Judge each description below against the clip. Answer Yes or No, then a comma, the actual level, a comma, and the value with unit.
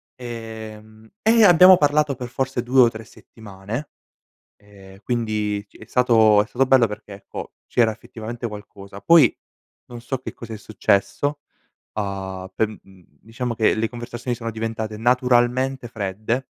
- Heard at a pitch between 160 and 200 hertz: No, low, 115 Hz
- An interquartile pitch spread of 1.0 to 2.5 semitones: No, average, 2.9 semitones